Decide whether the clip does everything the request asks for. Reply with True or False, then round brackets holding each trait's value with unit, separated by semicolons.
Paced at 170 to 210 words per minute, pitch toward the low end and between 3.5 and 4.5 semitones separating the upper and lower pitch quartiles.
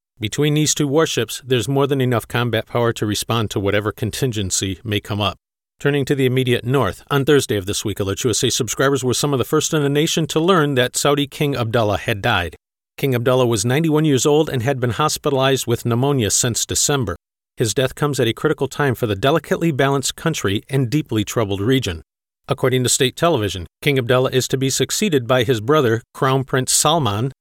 True (200 wpm; 130 Hz; 3.8 semitones)